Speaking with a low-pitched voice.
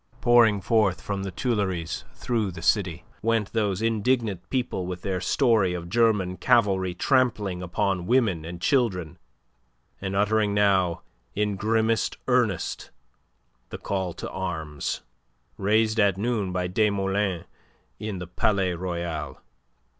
Yes: low, 100 Hz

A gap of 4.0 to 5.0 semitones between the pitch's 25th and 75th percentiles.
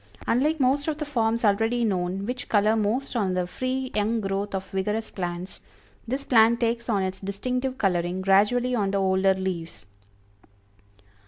Yes: average, 4.4 semitones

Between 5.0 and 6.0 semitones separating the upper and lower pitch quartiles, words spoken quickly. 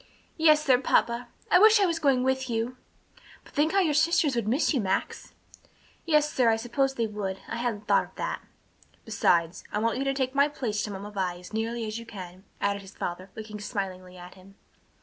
Yes: average, 5.3 semitones; fast, 210 wpm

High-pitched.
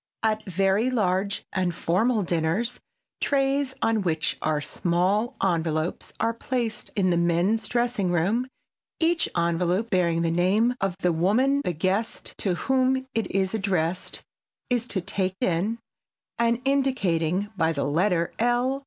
Yes: high, 195 Hz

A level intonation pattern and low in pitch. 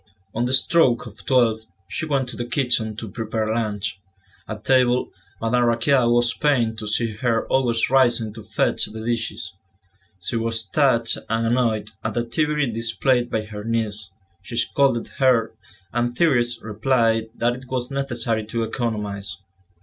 Yes: narrow, 2.1 semitones; low, 115 Hz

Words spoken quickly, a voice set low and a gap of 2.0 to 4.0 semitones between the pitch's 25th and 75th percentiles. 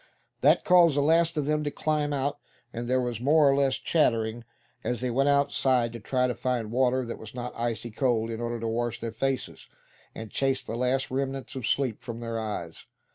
Yes: fast, 210 wpm; low, 125 Hz; average, 2.9 semitones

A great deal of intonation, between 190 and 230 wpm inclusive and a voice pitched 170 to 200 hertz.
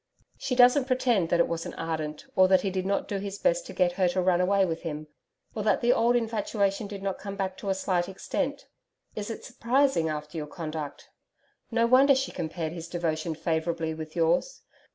Yes: wide, 5.7 semitones; fast, 205 wpm; high, 190 Hz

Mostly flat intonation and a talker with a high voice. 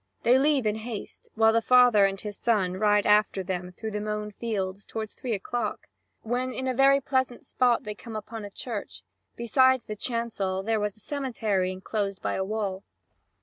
No: average, 3.2 semitones; high, 215 Hz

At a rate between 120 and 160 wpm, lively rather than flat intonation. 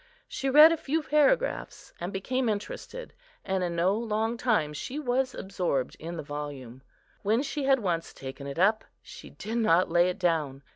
No: average, 180 wpm; wide, 7.6 semitones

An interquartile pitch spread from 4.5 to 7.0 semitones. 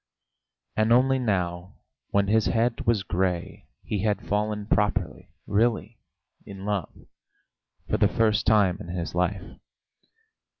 No: average, 2.8 semitones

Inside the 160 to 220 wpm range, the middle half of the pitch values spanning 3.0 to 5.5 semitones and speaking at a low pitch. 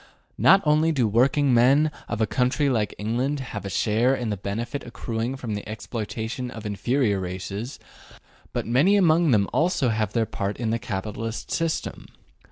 Yes: average, 175 wpm; average, 4.3 semitones; low, 115 Hz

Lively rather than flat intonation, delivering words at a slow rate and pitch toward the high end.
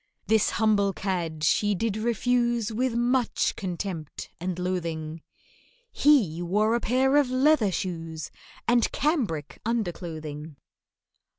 Yes: wide, 6.1 semitones; slow, 110 wpm; high, 205 Hz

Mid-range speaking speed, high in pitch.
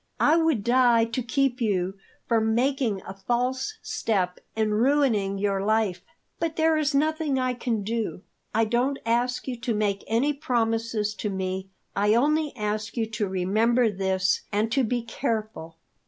Yes: average, 160 wpm; high, 225 Hz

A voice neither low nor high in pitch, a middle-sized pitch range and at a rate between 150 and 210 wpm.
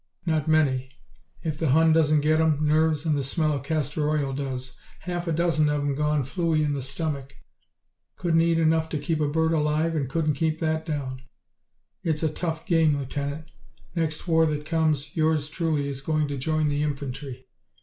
No: medium, 155 Hz; narrow, 2.0 semitones; average, 190 wpm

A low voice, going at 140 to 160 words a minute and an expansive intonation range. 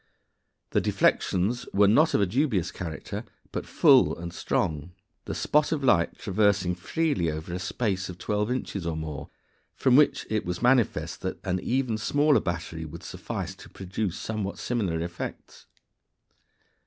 Yes: very low, 95 Hz; average, 155 wpm; wide, 5.8 semitones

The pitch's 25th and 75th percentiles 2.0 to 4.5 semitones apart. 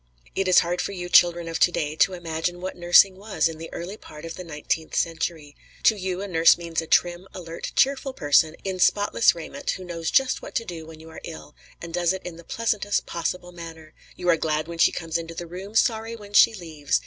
Yes: narrow, 2.6 semitones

